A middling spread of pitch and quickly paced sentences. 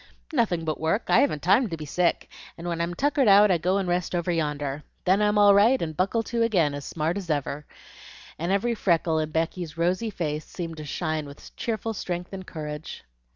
Yes: average, 4.2 semitones; fast, 210 wpm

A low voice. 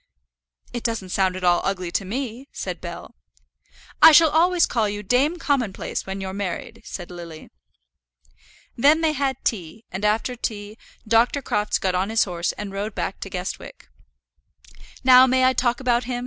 No: high, 220 Hz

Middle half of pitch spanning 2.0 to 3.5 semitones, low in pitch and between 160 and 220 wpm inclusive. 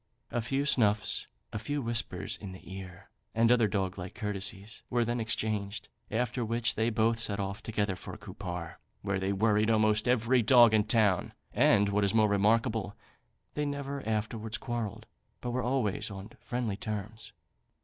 Yes: average, 2.7 semitones; low, 110 Hz; average, 170 wpm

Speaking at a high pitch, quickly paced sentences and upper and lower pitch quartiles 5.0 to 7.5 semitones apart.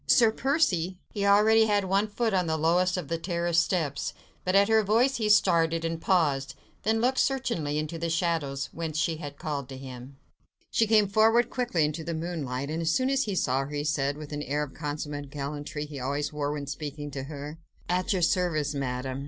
No: medium, 165 Hz; fast, 210 wpm; average, 5.3 semitones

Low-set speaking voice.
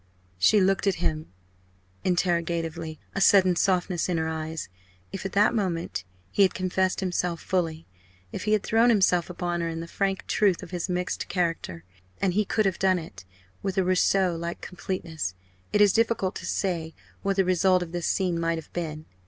No: medium, 180 Hz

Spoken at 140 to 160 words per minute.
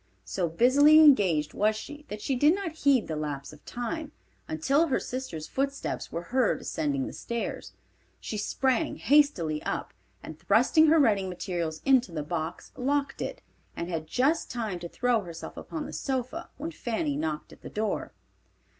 No: average, 170 wpm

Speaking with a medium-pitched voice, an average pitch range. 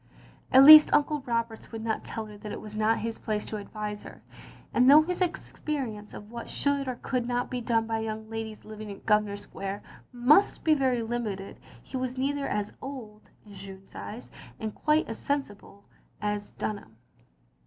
No: high, 225 Hz; average, 3.8 semitones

